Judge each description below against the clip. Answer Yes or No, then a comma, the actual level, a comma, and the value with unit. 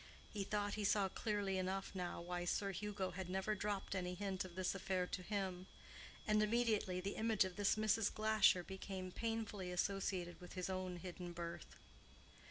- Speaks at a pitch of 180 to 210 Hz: Yes, high, 190 Hz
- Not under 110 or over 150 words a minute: No, average, 175 wpm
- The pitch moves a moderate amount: No, narrow, 2.3 semitones